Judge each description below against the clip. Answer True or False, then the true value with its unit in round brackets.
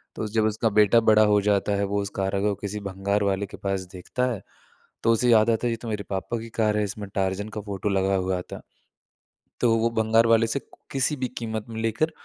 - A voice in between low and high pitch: False (105 Hz)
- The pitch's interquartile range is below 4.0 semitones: True (2.4 semitones)